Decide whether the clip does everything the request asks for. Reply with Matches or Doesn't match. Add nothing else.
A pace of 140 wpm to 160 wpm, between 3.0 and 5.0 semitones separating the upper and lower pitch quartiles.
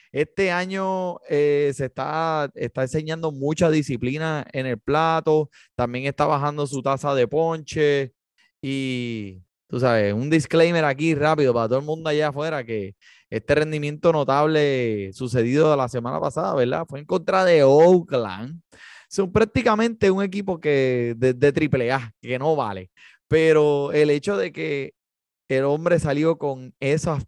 Matches